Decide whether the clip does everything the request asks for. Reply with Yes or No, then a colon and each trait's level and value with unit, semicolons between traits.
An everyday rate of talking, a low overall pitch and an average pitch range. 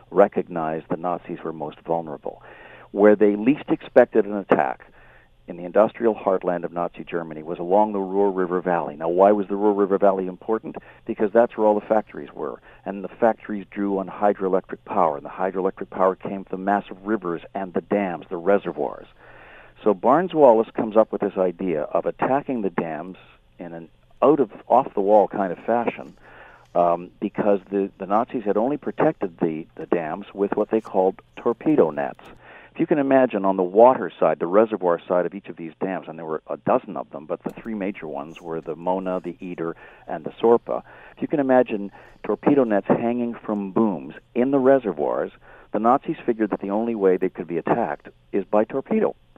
Yes: average, 195 wpm; low, 100 Hz; average, 3.2 semitones